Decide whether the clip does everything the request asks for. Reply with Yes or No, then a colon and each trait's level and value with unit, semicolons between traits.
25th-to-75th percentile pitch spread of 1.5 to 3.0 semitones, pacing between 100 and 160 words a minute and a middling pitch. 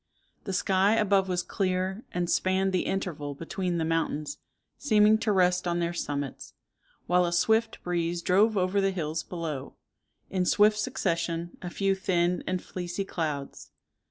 Yes: narrow, 2.4 semitones; average, 155 wpm; medium, 180 Hz